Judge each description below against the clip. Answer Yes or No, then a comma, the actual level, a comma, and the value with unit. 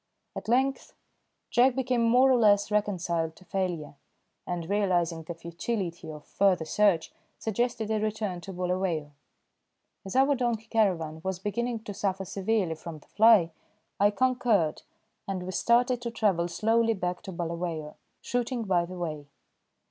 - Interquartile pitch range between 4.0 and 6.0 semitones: Yes, average, 4.9 semitones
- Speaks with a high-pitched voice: Yes, high, 195 Hz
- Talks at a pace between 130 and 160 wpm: Yes, average, 150 wpm